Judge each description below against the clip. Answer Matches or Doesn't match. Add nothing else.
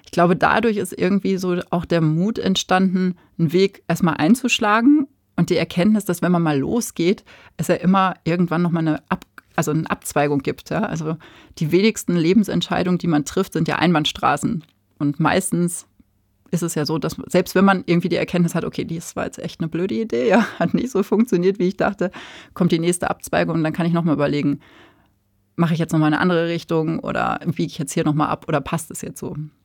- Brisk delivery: Matches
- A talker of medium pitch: Matches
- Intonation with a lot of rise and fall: Doesn't match